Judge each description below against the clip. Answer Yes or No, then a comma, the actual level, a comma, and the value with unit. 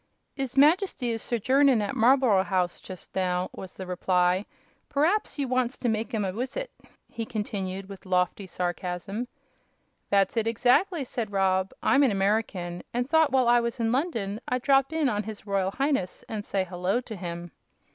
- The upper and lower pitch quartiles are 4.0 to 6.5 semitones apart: Yes, average, 5.3 semitones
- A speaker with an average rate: Yes, average, 175 wpm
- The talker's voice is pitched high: Yes, high, 220 Hz